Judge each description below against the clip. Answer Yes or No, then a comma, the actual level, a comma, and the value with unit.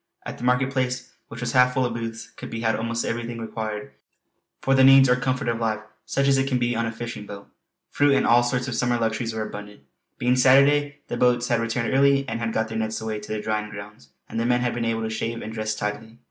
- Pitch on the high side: No, low, 115 Hz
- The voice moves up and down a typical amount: No, narrow, 2.2 semitones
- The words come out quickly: Yes, fast, 255 wpm